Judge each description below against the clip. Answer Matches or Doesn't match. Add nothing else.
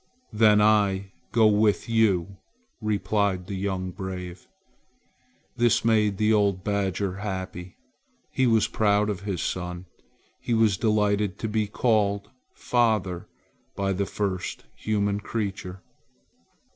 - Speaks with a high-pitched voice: Doesn't match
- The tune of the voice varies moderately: Doesn't match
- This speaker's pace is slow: Matches